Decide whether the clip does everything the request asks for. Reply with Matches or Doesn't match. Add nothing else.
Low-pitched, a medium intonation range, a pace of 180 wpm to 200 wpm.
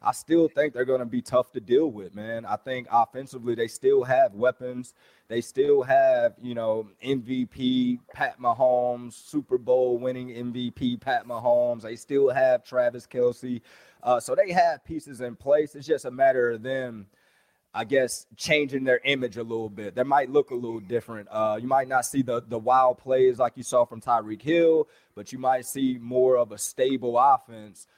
Matches